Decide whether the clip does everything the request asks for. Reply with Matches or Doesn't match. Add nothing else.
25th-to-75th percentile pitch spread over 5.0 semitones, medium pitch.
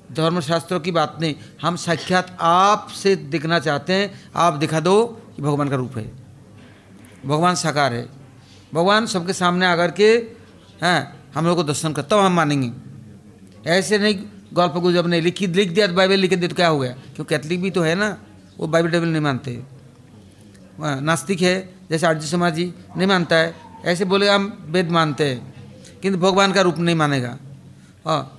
Doesn't match